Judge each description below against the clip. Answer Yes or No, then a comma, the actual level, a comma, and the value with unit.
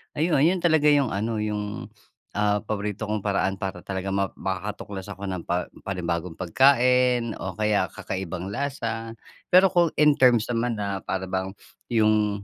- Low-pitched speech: Yes, low, 105 Hz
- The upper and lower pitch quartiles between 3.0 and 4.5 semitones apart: Yes, average, 4.2 semitones